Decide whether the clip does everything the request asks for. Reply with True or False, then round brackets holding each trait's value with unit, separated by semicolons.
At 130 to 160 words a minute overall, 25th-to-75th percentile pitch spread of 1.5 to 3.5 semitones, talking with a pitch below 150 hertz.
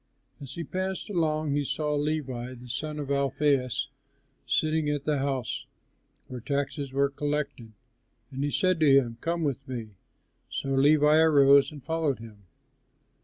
True (150 wpm; 2.4 semitones; 140 Hz)